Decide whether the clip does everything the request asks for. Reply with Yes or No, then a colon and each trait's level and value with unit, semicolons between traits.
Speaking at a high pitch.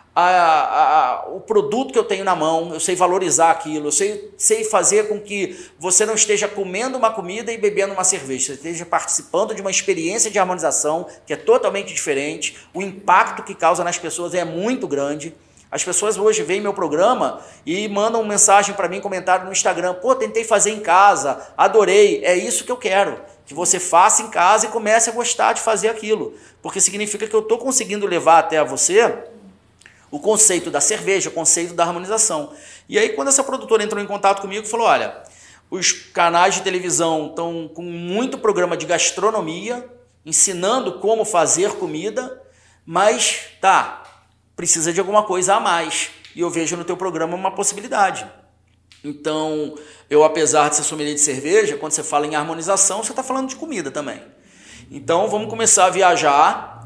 Yes: high, 195 Hz